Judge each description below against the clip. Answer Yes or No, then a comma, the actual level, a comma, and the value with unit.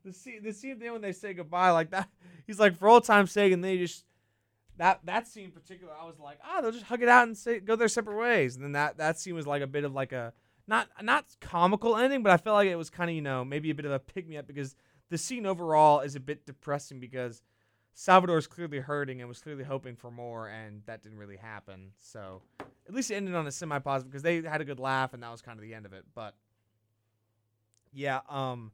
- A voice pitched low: No, medium, 145 Hz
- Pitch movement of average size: No, wide, 7.6 semitones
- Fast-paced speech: Yes, fast, 255 wpm